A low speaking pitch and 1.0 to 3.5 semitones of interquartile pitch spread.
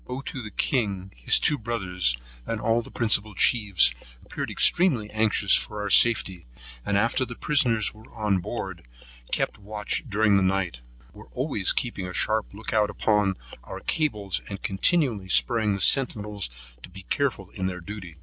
Yes: low, 105 Hz; average, 3.2 semitones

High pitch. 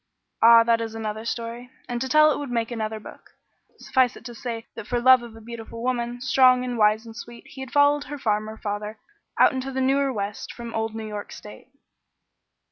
Yes: high, 235 Hz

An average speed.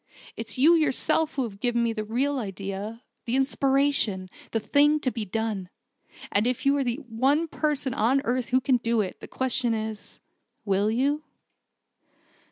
Yes: average, 170 wpm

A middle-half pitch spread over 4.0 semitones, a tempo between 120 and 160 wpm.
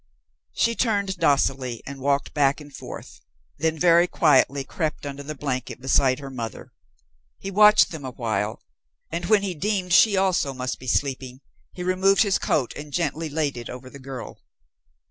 No: wide, 5.4 semitones; average, 170 wpm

